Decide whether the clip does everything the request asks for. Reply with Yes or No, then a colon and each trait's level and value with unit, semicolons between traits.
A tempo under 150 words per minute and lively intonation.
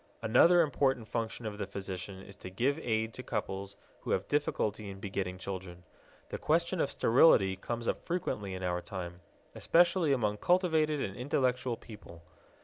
No: average, 160 wpm; wide, 6.7 semitones